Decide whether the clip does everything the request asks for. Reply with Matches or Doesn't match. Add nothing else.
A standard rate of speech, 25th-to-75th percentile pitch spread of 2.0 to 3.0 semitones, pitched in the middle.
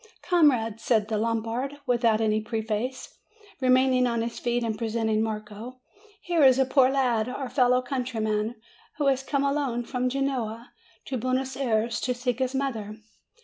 Doesn't match